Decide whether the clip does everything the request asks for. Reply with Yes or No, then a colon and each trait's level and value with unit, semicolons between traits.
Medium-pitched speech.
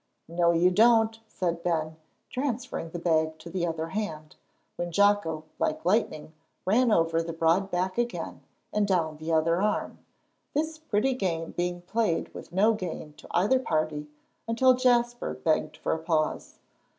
Yes: medium, 175 Hz